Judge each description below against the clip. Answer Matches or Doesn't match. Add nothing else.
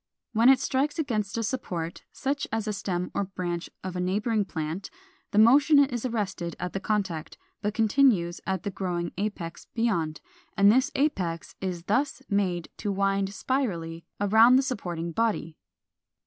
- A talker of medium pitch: Doesn't match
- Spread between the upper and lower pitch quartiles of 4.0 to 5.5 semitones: Matches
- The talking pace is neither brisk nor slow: Matches